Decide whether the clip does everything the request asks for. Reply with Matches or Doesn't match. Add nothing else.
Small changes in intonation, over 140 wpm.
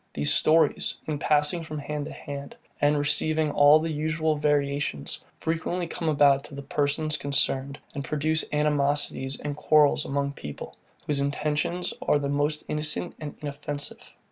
Matches